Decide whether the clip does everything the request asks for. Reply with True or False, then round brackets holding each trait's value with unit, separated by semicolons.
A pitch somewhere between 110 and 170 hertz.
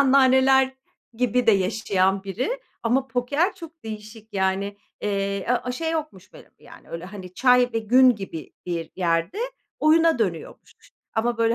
False (225 Hz)